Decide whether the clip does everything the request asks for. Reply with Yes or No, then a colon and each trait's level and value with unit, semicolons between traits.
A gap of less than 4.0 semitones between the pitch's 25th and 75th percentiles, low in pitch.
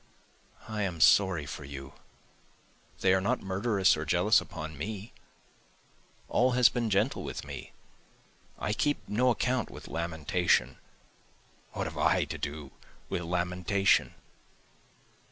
No: average, 5.3 semitones; very low, 95 Hz